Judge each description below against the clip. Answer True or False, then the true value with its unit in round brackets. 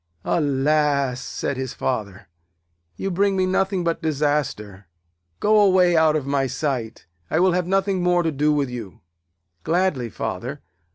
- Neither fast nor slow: True (150 wpm)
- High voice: False (150 Hz)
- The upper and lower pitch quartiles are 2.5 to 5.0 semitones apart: False (5.5 semitones)